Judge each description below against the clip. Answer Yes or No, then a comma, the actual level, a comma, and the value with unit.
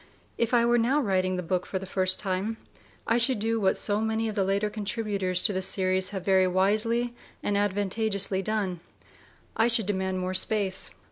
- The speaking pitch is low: No, high, 200 Hz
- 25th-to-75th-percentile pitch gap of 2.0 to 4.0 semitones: Yes, average, 2.9 semitones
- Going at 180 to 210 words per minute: Yes, average, 190 wpm